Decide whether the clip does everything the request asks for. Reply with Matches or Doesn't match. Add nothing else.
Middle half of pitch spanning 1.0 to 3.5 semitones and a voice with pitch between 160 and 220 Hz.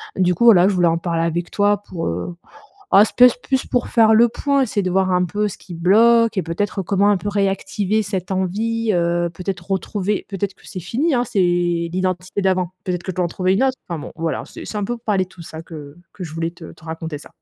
Matches